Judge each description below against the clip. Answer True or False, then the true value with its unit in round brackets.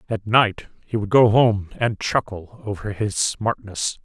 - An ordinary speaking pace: True (165 wpm)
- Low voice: True (105 Hz)